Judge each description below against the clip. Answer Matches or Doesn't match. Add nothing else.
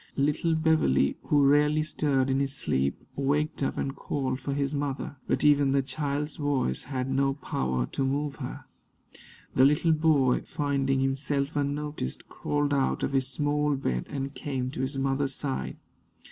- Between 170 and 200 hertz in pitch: Doesn't match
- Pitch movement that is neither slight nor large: Doesn't match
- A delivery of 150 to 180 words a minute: Matches